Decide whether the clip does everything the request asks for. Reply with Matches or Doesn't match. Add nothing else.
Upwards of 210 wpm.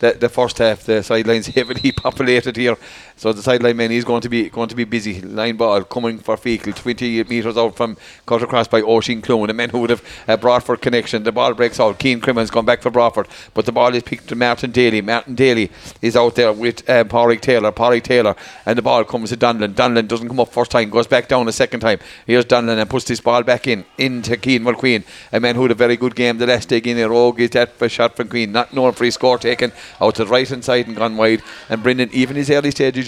Matches